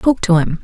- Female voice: Yes, female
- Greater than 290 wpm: No, fast, 285 wpm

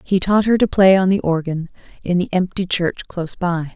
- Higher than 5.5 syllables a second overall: No, 5.1 syllables/s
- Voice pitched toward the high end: No, medium, 180 Hz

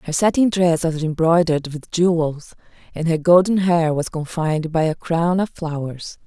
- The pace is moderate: Yes, average, 170 wpm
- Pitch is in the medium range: Yes, medium, 165 Hz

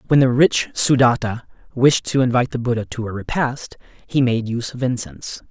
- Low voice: Yes, low, 120 Hz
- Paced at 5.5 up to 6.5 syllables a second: Yes, 5.6 syllables/s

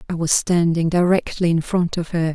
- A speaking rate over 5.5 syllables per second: No, 5.1 syllables/s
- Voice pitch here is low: No, medium, 170 Hz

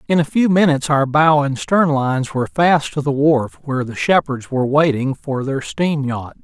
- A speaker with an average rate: No, fast, 215 wpm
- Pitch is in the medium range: Yes, medium, 145 Hz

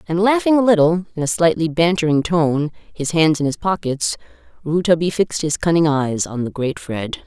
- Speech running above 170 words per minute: Yes, average, 190 wpm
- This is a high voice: No, medium, 165 Hz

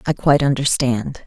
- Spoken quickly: No, average, 140 wpm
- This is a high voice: No, low, 135 Hz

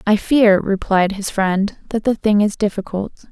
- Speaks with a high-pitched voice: Yes, high, 205 Hz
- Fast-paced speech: No, average, 180 wpm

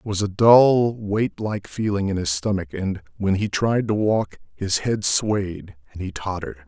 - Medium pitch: No, low, 100 Hz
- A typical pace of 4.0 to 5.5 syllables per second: Yes, 4.6 syllables/s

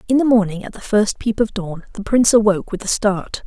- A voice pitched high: Yes, high, 210 Hz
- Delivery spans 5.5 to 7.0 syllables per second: Yes, 6.0 syllables/s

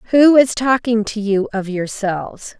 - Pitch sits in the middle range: No, high, 220 Hz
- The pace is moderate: Yes, average, 160 wpm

